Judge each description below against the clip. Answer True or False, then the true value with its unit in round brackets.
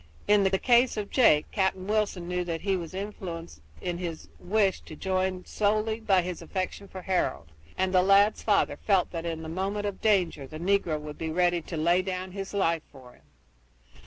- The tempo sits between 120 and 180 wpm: False (195 wpm)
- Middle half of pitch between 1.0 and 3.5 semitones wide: True (3.0 semitones)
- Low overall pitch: False (185 Hz)